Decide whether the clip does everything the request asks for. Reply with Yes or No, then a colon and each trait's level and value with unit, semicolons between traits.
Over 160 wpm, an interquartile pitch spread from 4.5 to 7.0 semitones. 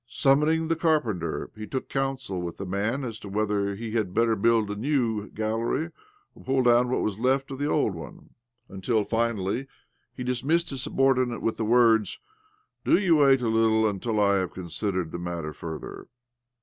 Yes: average, 185 wpm; average, 4.9 semitones